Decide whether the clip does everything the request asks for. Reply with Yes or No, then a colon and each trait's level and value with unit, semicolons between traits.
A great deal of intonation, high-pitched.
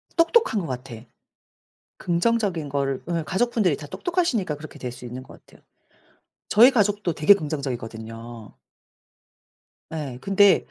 No: wide, 8.0 semitones; medium, 160 Hz